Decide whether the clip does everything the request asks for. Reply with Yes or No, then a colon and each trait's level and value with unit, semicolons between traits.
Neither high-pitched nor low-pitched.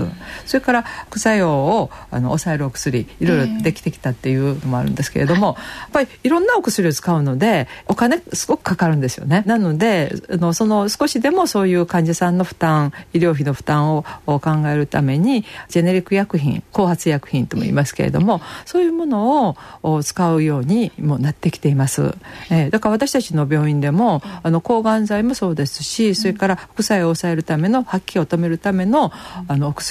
Yes: medium, 175 Hz